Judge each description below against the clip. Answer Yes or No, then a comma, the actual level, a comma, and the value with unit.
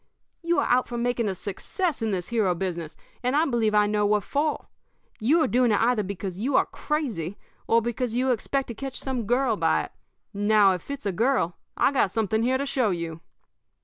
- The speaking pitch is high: Yes, high, 230 Hz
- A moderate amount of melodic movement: Yes, average, 4.4 semitones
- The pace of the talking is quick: Yes, fast, 215 wpm